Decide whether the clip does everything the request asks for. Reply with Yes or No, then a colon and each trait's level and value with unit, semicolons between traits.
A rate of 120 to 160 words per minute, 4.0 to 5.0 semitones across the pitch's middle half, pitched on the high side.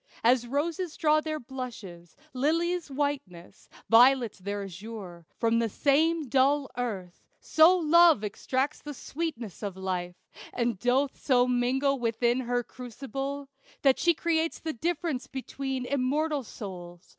Yes: slow, 135 wpm; average, 4.5 semitones; very high, 260 Hz